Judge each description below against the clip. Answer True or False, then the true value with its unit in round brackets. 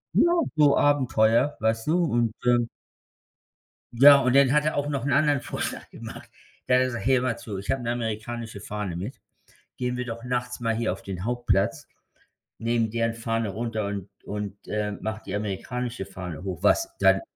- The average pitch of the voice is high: False (115 Hz)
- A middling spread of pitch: True (3.1 semitones)